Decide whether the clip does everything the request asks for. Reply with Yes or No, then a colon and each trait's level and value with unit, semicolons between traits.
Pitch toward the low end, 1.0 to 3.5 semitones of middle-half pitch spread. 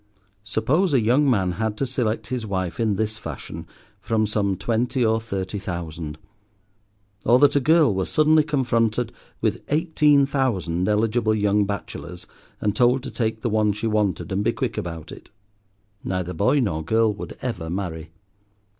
No: low, 110 Hz; average, 4.6 semitones